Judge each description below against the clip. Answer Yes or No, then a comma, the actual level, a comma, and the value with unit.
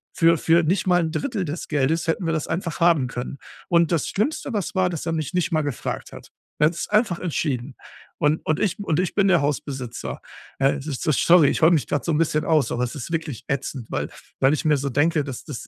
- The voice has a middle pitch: Yes, medium, 160 Hz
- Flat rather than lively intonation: No, average, 3.1 semitones